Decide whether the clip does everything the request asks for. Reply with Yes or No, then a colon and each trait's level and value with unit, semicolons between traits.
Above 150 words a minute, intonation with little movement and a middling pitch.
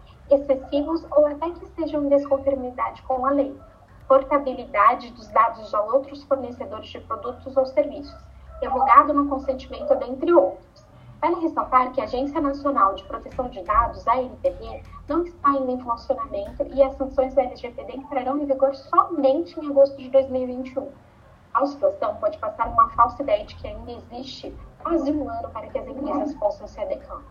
No: average, 165 wpm; narrow, 2.2 semitones; very high, 275 Hz